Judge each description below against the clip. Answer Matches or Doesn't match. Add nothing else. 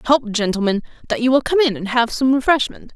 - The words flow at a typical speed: Doesn't match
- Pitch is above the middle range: Matches